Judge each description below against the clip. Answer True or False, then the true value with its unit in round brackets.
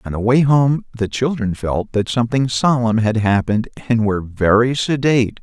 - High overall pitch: False (115 Hz)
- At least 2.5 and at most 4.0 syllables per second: False (5.2 syllables/s)